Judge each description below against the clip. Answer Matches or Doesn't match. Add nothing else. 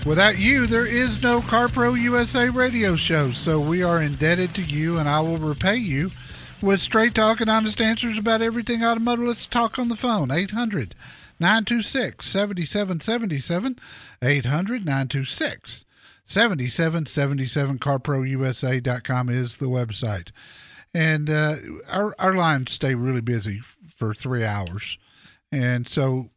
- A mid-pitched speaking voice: Matches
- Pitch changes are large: Matches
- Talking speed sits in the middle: Doesn't match